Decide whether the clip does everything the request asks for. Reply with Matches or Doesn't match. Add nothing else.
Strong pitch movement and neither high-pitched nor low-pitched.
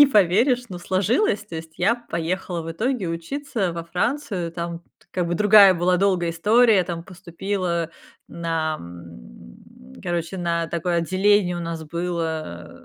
Doesn't match